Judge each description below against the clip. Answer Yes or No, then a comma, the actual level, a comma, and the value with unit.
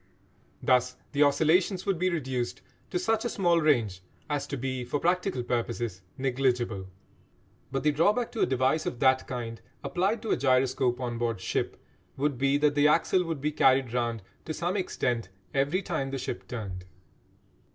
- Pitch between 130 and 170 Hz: Yes, low, 135 Hz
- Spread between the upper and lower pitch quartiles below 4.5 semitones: No, average, 5.0 semitones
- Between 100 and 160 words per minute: No, average, 170 wpm